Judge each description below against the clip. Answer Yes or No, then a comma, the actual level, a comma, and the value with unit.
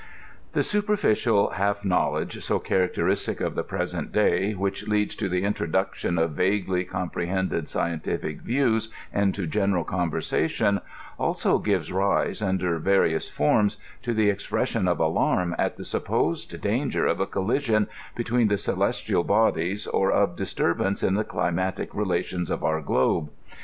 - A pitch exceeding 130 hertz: No, very low, 95 Hz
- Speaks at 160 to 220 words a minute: No, average, 140 wpm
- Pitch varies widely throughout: No, average, 2.9 semitones